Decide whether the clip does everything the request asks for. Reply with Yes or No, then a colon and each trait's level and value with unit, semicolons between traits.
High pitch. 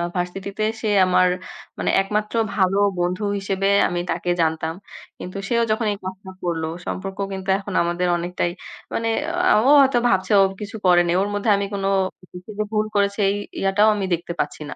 Yes: high, 195 Hz